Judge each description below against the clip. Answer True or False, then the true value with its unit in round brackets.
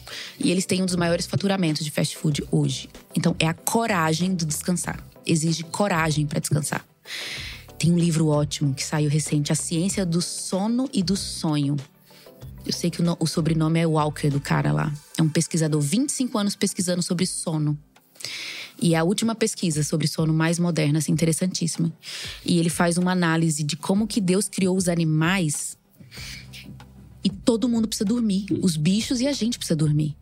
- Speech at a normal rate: True (175 wpm)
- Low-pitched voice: False (165 Hz)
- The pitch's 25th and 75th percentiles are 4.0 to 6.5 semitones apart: False (3.5 semitones)